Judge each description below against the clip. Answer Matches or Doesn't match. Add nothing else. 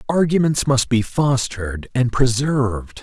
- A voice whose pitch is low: Matches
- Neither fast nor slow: Doesn't match